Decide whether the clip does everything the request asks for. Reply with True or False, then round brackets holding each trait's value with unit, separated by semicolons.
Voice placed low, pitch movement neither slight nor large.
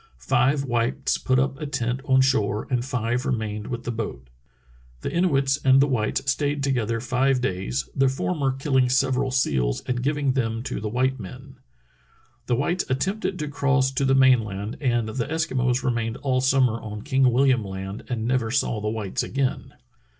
True (130 Hz; 3.1 semitones)